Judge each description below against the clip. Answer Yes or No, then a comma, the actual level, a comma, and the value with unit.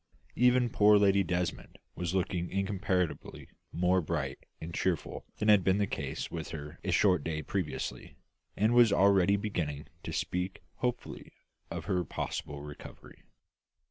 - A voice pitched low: Yes, very low, 90 Hz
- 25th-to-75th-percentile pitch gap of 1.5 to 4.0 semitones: Yes, average, 3.4 semitones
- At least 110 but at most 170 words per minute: Yes, average, 140 wpm